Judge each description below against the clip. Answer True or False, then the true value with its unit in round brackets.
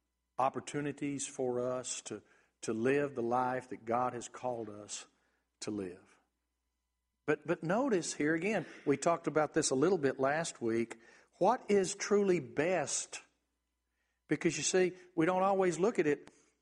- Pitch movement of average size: False (6.4 semitones)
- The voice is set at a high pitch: False (135 Hz)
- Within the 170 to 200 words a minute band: False (150 wpm)